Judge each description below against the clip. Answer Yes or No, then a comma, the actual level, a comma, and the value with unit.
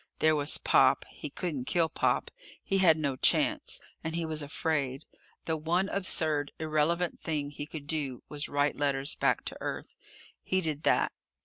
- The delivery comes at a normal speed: Yes, average, 170 wpm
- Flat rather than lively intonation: Yes, narrow, 2.2 semitones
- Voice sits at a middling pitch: Yes, medium, 155 Hz